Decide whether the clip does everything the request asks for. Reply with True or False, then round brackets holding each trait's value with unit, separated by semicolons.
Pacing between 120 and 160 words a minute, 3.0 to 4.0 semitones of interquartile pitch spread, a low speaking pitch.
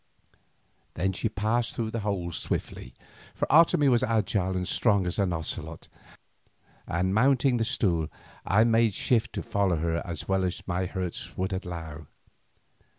False (150 wpm; 4.4 semitones; 95 Hz)